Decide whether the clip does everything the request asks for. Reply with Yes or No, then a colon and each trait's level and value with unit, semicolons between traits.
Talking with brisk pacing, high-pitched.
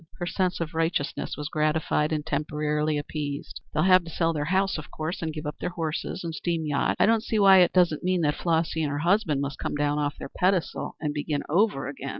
No: fast, 230 wpm; medium, 160 Hz